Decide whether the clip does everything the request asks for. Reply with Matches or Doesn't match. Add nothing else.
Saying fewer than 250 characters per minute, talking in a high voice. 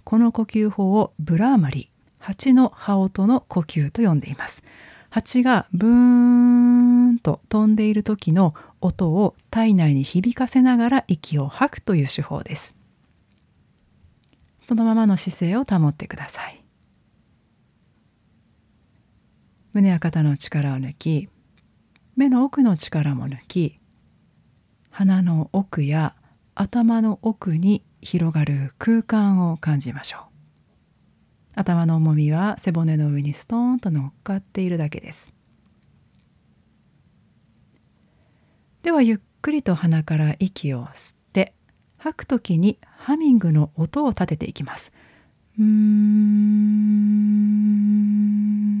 Matches